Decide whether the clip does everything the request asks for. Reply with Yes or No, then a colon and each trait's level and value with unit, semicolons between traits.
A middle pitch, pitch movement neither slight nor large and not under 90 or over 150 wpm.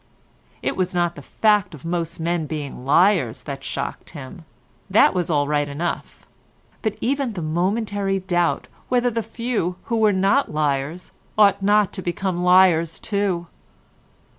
Yes: medium, 180 Hz; average, 4.5 semitones; average, 145 wpm